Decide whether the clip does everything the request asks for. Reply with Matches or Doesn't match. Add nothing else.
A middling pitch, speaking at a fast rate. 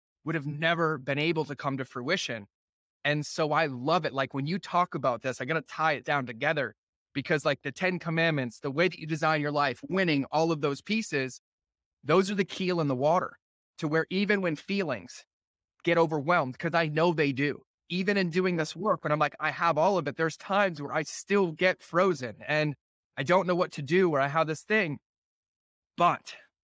Matches